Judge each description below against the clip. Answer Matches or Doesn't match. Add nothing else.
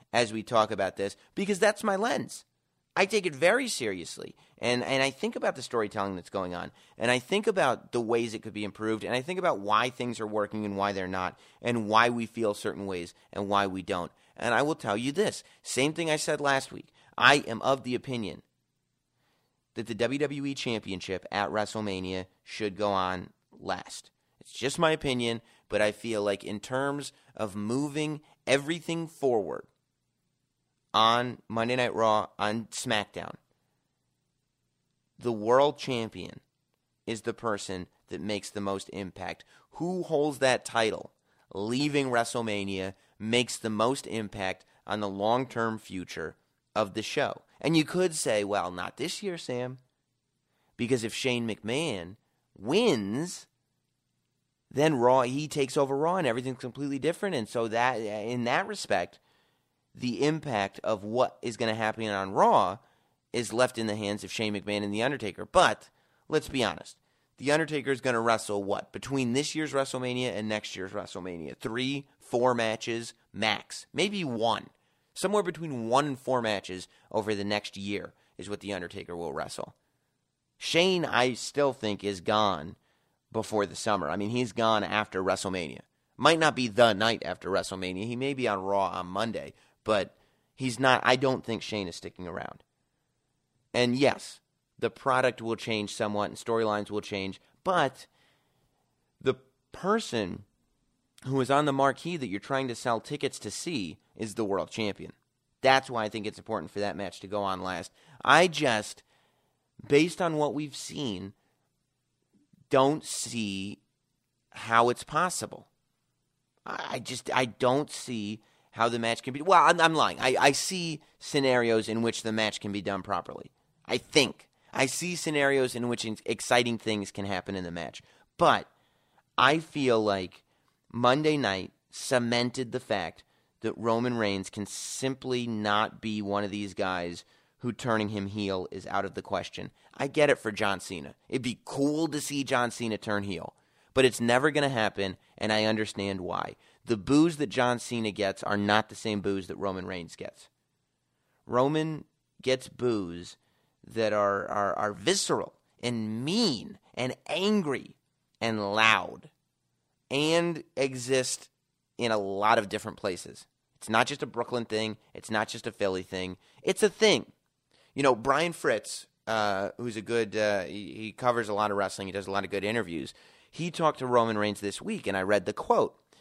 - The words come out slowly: Doesn't match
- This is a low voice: Matches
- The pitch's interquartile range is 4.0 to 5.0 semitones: Matches